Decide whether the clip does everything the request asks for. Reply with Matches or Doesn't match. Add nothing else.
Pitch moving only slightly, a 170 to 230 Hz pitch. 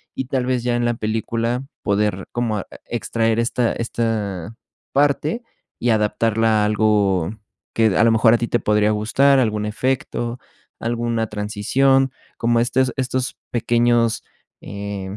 Doesn't match